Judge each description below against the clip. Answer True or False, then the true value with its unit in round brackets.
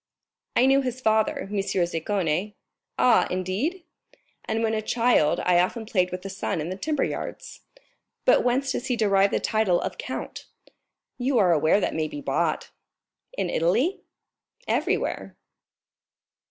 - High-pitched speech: True (210 Hz)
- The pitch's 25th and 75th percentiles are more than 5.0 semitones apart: True (5.5 semitones)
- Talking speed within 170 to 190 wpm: False (150 wpm)